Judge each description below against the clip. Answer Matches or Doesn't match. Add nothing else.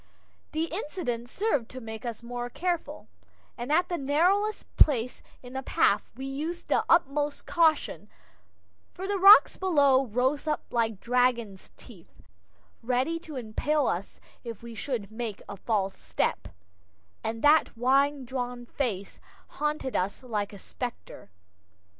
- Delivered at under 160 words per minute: Matches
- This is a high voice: Matches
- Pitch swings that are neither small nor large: Matches